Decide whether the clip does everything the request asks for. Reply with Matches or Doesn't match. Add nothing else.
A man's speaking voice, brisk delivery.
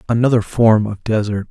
Doesn't match